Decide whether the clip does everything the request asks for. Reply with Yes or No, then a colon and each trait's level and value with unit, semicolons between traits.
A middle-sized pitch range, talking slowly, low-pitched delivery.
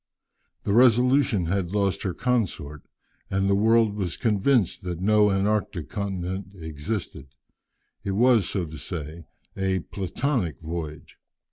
Yes: average, 3.8 semitones; slow, 125 wpm; very low, 95 Hz